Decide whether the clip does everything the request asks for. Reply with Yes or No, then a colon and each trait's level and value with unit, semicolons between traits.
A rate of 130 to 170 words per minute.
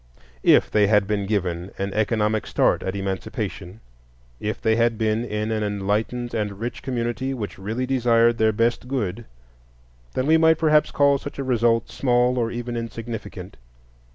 Yes: average, 160 wpm